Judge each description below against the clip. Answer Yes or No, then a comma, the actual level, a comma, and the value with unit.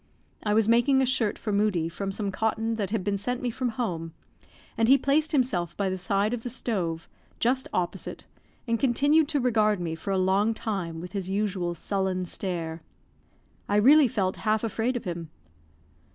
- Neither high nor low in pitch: No, high, 210 Hz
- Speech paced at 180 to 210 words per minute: Yes, average, 185 wpm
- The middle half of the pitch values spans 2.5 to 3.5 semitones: No, average, 4.5 semitones